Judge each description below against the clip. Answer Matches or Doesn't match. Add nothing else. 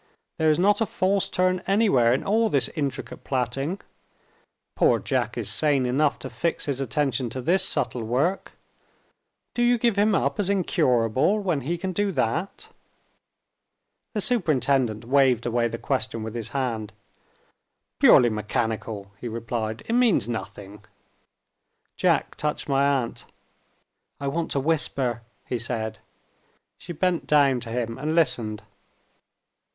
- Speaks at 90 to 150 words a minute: Matches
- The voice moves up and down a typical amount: Doesn't match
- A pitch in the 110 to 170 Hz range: Matches